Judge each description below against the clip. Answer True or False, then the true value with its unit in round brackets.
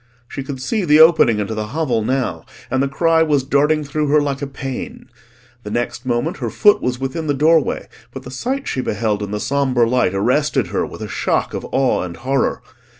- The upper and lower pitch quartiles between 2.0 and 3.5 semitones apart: False (4.0 semitones)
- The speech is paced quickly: True (210 wpm)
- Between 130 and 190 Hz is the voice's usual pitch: True (135 Hz)